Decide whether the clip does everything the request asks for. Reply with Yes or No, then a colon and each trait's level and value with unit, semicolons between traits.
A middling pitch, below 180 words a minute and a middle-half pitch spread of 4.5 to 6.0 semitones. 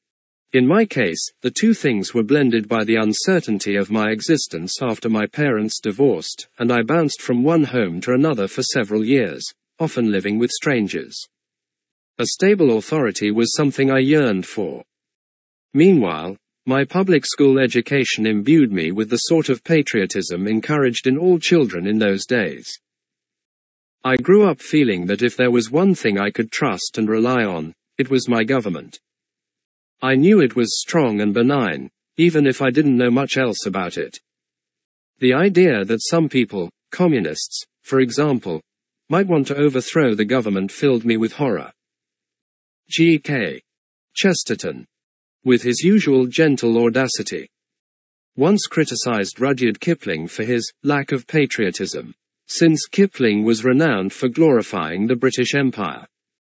No: low, 130 Hz; average, 150 wpm; average, 5.2 semitones